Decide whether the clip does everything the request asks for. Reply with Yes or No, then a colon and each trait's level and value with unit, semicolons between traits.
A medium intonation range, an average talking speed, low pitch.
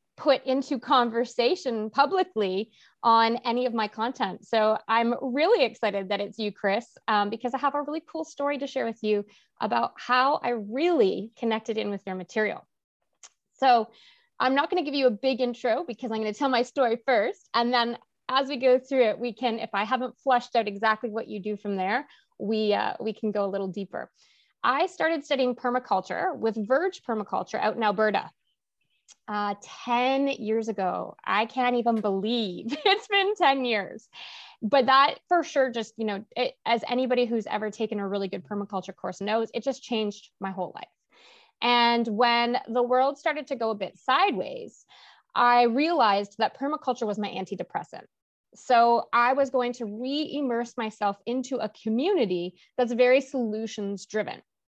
No: average, 3.5 semitones; average, 180 wpm; high, 235 Hz